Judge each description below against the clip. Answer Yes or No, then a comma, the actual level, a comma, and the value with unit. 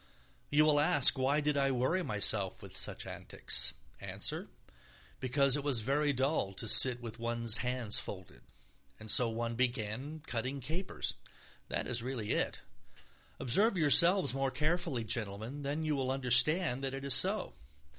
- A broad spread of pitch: No, average, 3.8 semitones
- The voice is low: Yes, low, 130 Hz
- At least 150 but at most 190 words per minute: Yes, average, 155 wpm